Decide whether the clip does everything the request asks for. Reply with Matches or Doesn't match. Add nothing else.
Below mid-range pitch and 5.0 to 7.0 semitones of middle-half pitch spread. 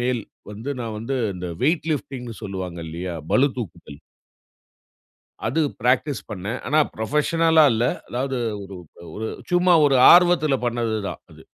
Matches